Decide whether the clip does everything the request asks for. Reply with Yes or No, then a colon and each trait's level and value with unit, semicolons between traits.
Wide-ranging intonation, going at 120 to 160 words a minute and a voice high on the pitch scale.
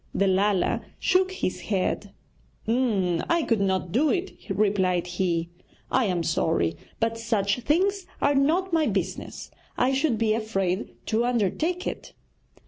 Yes: wide, 7.2 semitones; slow, 135 wpm; high, 220 Hz